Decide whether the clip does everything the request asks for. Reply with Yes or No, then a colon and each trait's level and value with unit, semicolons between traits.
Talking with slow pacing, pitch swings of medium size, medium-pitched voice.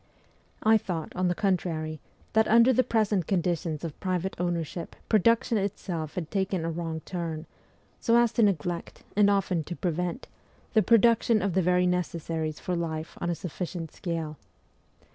No: average, 160 wpm; average, 3.6 semitones; medium, 180 Hz